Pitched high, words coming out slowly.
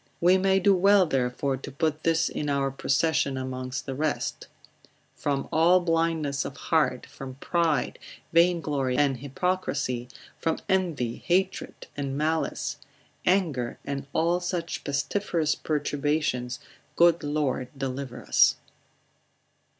No: medium, 150 Hz; slow, 120 wpm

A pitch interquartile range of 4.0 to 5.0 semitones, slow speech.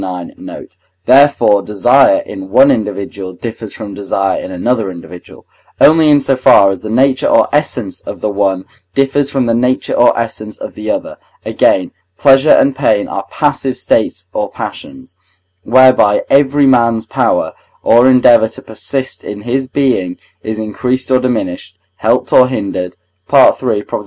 No: average, 4.6 semitones; average, 155 wpm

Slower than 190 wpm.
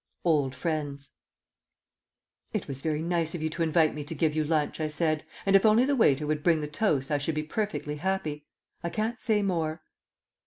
No: average, 200 wpm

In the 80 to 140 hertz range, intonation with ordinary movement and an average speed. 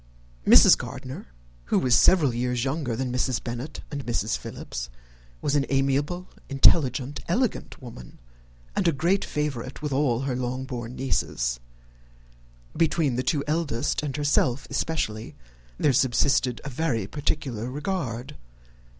No: low, 135 Hz; average, 3.5 semitones; slow, 125 wpm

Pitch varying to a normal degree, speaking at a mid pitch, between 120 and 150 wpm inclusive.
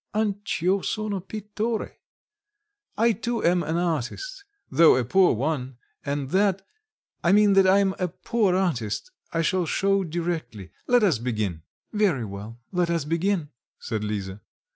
No: wide, 7.2 semitones; medium, 175 Hz; average, 145 wpm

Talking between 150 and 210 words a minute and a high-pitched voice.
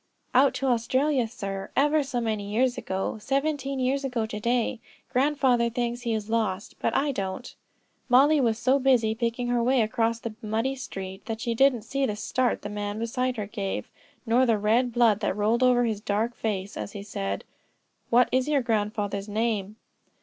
Yes: average, 185 wpm; high, 235 Hz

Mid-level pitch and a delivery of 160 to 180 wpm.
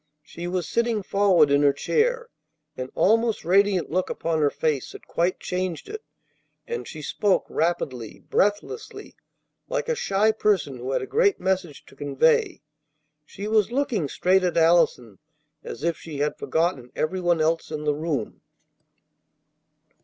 No: medium, 175 Hz; average, 150 wpm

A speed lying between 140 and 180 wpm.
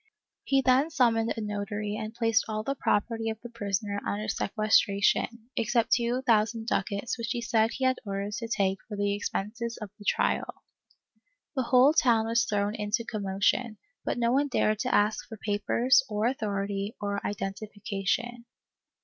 Yes: average, 165 wpm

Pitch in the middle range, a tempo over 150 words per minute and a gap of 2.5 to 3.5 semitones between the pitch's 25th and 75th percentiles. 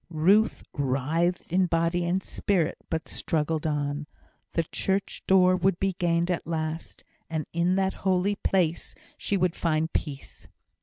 No: medium, 170 Hz; average, 145 wpm; average, 2.8 semitones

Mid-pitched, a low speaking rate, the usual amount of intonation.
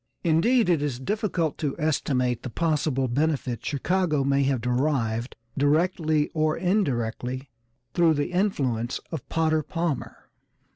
Yes: medium, 150 Hz; slow, 125 wpm; average, 4.3 semitones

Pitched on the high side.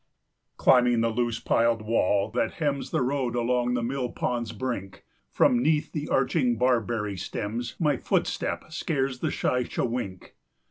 No: low, 120 Hz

